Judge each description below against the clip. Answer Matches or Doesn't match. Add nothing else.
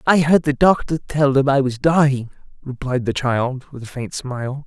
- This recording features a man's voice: Matches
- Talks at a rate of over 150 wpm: Matches